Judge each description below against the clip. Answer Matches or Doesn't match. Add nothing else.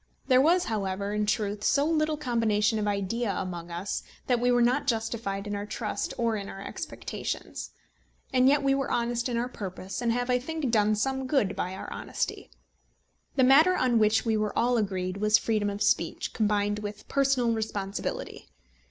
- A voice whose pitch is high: Matches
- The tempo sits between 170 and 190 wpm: Matches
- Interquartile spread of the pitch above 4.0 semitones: Doesn't match